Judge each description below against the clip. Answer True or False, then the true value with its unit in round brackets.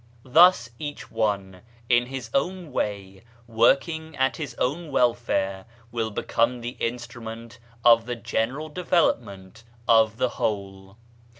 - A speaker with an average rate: False (120 wpm)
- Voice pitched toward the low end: True (120 Hz)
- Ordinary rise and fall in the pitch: True (3.2 semitones)